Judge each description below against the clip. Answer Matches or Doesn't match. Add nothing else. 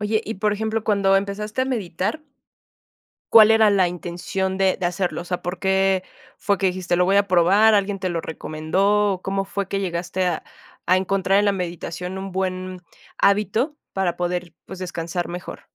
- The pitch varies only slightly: Matches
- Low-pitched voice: Doesn't match